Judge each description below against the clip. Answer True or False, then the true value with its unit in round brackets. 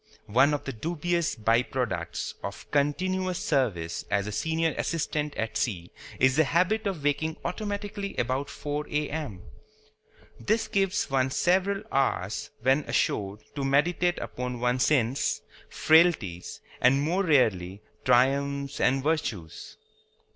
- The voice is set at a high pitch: False (140 Hz)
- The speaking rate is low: True (125 wpm)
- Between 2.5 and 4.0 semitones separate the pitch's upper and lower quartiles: False (5.4 semitones)